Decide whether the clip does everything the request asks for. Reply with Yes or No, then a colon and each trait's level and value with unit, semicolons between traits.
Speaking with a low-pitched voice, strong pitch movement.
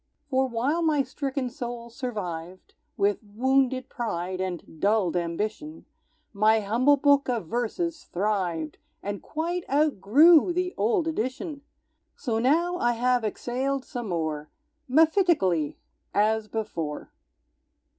No: high, 240 Hz; wide, 6.0 semitones